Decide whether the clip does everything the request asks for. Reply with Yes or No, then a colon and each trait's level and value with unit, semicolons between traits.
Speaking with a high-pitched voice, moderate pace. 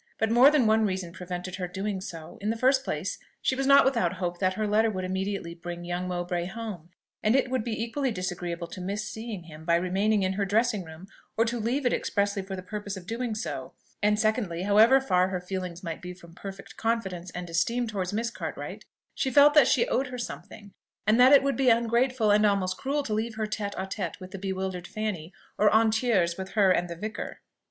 No: high, 205 Hz; fast, 225 wpm